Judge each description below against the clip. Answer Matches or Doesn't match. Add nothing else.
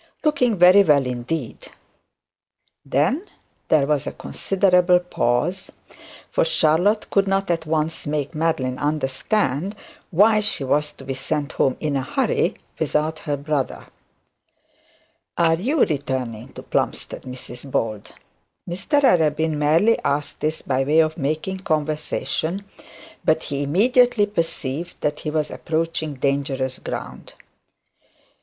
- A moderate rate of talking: Doesn't match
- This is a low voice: Doesn't match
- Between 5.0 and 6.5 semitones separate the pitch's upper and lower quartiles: Doesn't match